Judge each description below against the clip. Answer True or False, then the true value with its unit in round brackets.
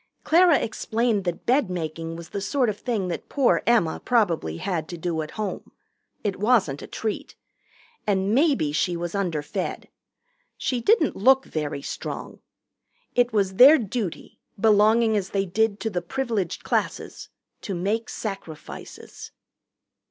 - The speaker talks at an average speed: True (145 wpm)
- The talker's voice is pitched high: True (205 Hz)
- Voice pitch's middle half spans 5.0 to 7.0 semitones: True (5.3 semitones)